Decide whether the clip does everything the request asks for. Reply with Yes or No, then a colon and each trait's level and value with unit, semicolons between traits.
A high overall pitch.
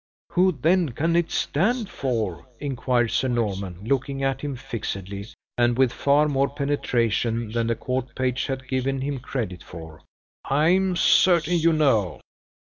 No: low, 130 Hz